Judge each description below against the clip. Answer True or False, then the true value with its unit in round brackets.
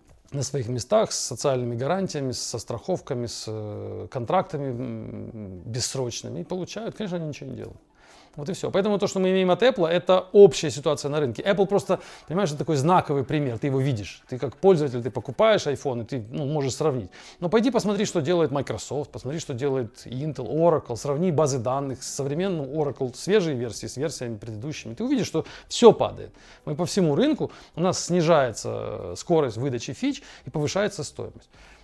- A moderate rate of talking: True (175 wpm)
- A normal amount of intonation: False (6.3 semitones)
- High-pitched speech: False (150 Hz)